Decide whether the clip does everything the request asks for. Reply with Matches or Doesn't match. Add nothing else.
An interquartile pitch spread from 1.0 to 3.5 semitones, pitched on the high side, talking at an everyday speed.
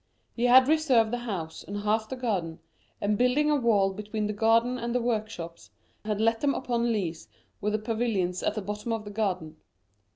Matches